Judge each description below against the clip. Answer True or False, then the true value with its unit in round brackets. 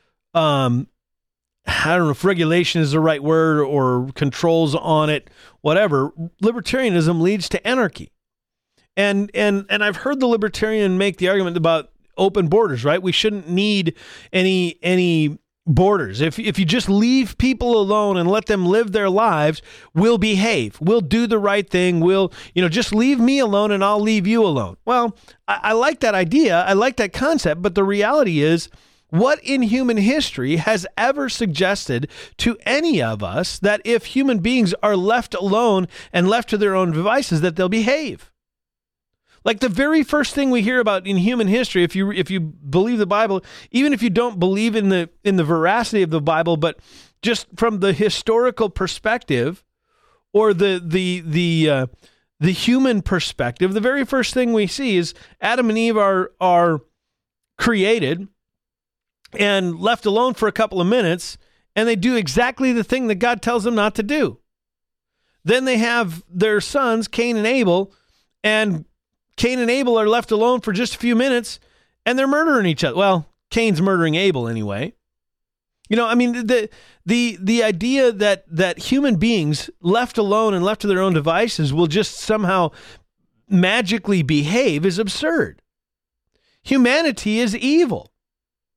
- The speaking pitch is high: True (205 Hz)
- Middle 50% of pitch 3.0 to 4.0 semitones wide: False (4.9 semitones)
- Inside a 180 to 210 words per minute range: False (170 wpm)